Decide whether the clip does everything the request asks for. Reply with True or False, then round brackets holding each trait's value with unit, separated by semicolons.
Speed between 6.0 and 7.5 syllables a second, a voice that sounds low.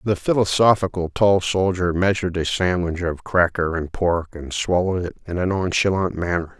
False (5.1 syllables/s; 90 Hz)